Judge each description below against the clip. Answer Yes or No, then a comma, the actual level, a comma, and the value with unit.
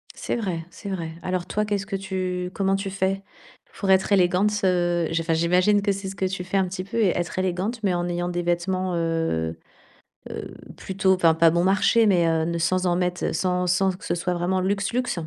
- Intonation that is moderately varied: No, narrow, 1.9 semitones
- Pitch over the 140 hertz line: Yes, medium, 185 Hz